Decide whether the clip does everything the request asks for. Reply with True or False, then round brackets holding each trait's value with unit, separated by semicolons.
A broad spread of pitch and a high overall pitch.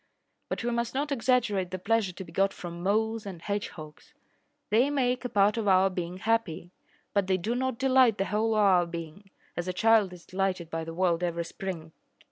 False (4.3 semitones; 195 Hz)